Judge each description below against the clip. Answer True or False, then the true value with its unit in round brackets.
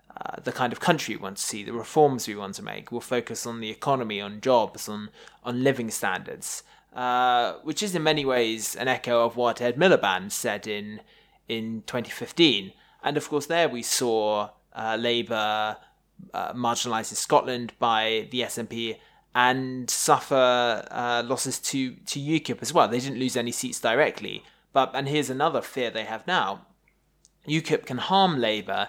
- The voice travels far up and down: False (3.2 semitones)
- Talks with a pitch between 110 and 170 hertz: True (120 Hz)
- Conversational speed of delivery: True (175 wpm)